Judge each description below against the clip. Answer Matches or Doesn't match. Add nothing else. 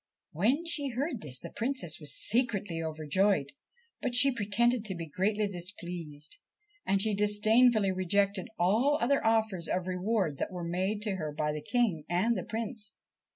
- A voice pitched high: Matches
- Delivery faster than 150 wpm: Matches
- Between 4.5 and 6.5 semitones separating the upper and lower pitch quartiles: Matches